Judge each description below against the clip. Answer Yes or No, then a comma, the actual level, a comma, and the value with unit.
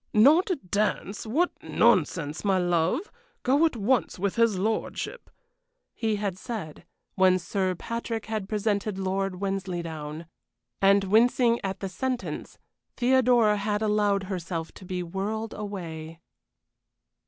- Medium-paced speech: No, slow, 120 wpm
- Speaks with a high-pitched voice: Yes, high, 200 Hz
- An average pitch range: Yes, average, 3.3 semitones